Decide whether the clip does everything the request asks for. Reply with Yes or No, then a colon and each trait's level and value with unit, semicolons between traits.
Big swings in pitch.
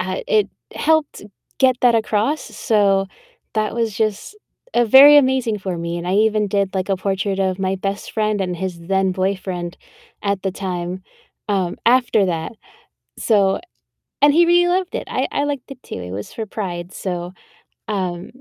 No: average, 4.2 semitones